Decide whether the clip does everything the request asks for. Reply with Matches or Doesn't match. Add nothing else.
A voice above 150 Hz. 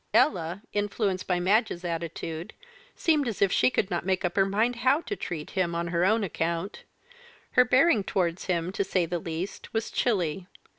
Matches